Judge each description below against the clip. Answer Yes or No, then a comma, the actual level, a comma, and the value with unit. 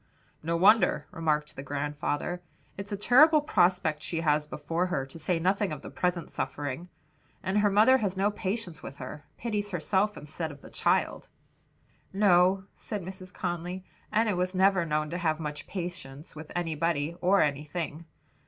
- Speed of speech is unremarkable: Yes, average, 160 wpm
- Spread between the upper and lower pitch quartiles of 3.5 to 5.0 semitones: Yes, average, 4.1 semitones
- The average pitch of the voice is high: No, medium, 175 Hz